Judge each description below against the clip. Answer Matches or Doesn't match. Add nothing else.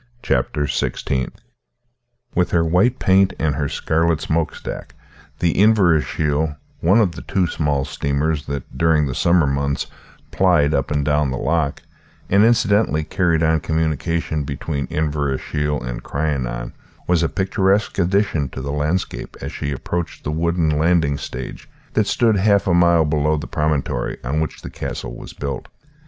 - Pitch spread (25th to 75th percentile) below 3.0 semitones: Doesn't match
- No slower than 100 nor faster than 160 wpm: Matches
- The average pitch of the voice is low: Matches